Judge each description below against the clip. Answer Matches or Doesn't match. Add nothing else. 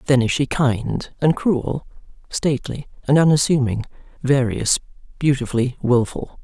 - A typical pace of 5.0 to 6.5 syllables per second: Doesn't match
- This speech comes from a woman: Matches